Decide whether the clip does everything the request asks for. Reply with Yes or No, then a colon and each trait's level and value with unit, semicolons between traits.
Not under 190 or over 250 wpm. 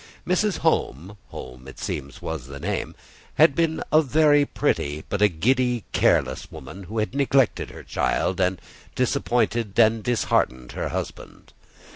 No: average, 145 wpm